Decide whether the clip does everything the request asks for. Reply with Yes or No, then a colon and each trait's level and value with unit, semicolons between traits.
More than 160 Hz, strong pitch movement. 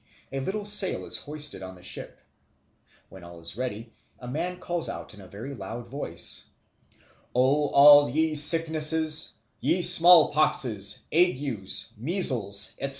No: medium, 140 Hz; wide, 6.4 semitones